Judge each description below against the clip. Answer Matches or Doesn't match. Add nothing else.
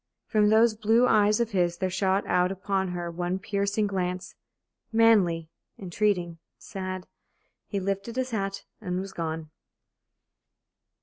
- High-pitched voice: Matches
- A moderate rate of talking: Doesn't match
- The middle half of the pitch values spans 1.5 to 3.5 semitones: Matches